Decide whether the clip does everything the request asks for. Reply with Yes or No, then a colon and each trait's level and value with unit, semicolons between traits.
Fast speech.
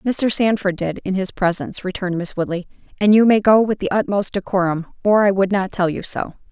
Yes: fast, 220 wpm